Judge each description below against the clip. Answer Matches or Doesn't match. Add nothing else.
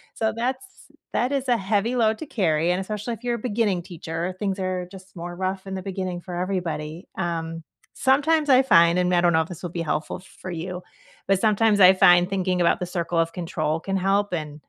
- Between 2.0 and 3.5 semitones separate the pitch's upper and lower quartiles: Matches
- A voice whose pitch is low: Doesn't match